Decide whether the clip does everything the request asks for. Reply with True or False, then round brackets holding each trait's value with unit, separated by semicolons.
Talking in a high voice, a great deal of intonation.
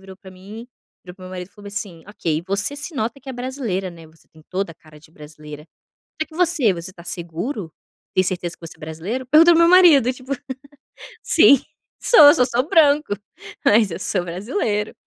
True (200 Hz; 7.3 semitones)